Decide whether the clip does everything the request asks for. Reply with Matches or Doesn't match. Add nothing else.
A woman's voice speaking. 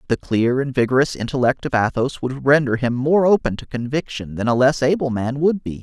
Doesn't match